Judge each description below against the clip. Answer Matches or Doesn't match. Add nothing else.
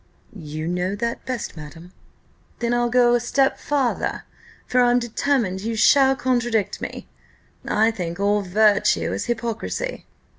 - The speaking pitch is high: Matches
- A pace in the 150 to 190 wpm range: Doesn't match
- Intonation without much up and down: Doesn't match